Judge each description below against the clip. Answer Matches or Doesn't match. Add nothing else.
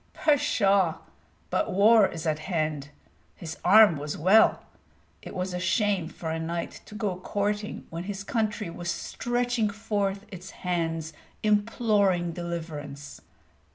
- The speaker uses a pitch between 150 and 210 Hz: Matches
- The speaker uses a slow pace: Matches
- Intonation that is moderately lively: Matches